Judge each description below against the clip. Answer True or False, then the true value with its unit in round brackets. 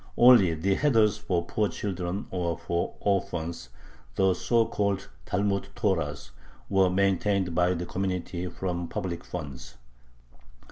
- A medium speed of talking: False (125 wpm)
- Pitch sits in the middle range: False (90 Hz)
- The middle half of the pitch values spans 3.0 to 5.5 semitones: False (2.4 semitones)